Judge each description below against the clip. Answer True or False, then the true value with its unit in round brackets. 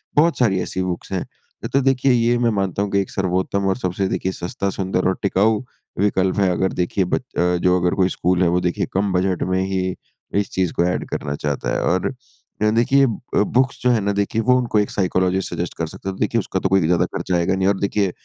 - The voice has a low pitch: True (95 Hz)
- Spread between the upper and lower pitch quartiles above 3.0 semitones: False (2.5 semitones)